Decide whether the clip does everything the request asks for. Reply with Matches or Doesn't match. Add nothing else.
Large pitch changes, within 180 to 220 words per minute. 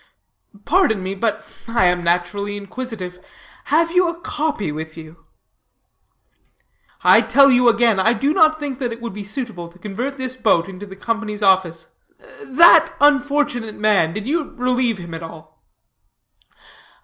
Doesn't match